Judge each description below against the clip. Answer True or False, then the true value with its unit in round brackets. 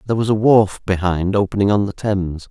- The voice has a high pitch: False (100 Hz)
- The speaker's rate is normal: False (215 wpm)